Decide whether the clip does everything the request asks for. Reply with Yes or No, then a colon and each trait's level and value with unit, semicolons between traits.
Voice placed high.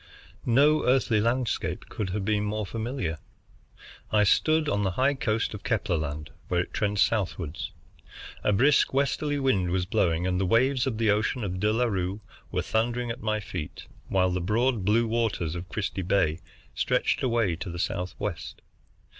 No: low, 105 Hz